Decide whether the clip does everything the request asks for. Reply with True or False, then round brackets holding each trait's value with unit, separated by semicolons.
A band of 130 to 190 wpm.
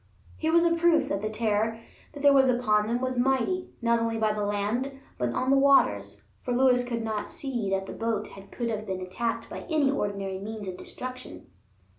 False (200 wpm)